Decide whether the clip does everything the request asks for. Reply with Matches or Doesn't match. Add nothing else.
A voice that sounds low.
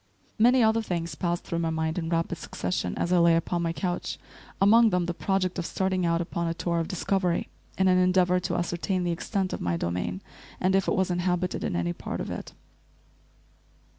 Doesn't match